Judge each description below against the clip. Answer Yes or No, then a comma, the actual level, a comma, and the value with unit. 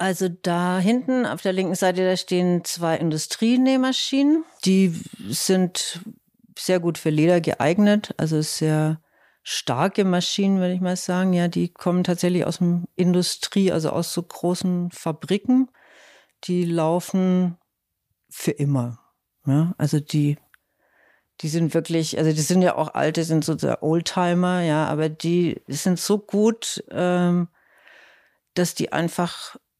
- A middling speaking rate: Yes, average, 135 wpm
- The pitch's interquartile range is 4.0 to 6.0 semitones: No, narrow, 2.6 semitones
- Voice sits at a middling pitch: Yes, medium, 175 Hz